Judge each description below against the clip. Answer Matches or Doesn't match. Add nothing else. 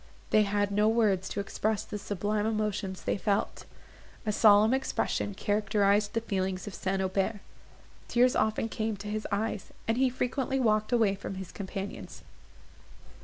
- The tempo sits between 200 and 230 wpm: Doesn't match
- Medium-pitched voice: Doesn't match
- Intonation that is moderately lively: Doesn't match